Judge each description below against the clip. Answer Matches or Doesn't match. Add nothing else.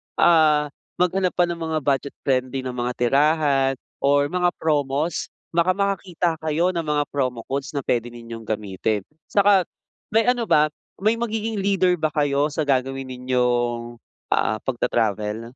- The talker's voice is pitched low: Doesn't match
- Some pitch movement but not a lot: Doesn't match